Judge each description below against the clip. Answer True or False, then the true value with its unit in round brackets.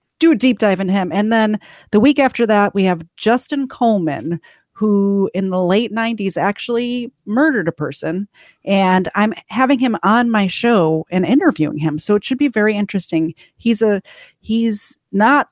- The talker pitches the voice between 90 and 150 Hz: False (210 Hz)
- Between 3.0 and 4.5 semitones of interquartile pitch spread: True (3.8 semitones)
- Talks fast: False (175 wpm)